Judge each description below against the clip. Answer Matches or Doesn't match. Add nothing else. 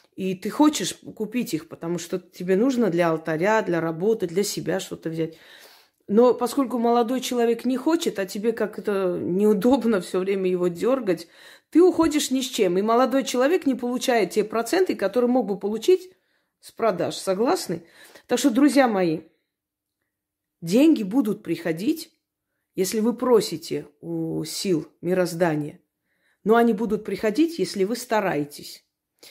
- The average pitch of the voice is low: Doesn't match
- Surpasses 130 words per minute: Matches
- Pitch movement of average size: Doesn't match